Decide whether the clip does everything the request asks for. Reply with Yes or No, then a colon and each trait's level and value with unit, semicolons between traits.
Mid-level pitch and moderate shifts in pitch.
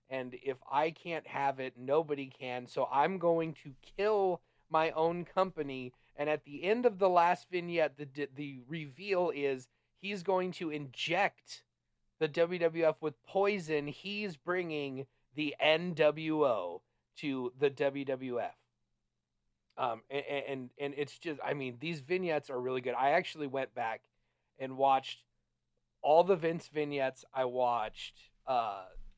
Yes: medium, 145 Hz; average, 4.3 semitones